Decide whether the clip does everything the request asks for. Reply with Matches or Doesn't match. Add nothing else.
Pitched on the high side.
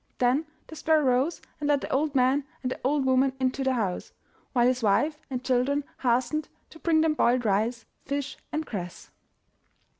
Matches